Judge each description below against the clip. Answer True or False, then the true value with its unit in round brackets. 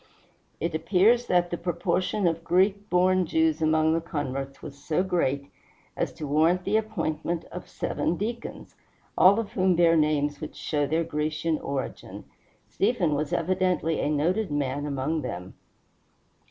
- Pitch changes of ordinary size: True (3.5 semitones)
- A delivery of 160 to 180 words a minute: False (150 wpm)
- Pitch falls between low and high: True (165 Hz)